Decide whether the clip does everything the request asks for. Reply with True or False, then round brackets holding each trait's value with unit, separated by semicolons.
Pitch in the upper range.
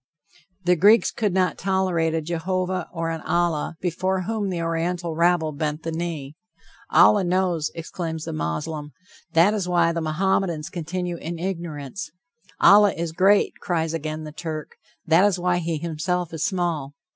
False (170 Hz)